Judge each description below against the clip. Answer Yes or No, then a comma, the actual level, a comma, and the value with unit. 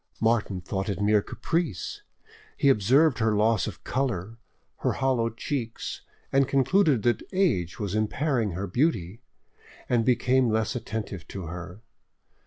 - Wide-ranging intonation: No, average, 4.7 semitones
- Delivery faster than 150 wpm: No, slow, 135 wpm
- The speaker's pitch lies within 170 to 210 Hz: No, low, 115 Hz